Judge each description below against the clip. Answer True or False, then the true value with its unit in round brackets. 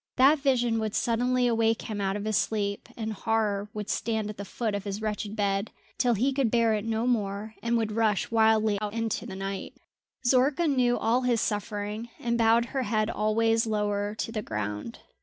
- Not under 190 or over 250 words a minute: True (195 wpm)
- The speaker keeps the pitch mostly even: True (2.2 semitones)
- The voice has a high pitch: True (220 Hz)